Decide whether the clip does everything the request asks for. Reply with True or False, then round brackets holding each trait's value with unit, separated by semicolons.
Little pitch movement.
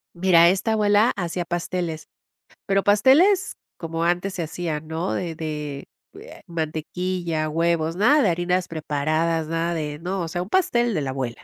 False (3.0 semitones)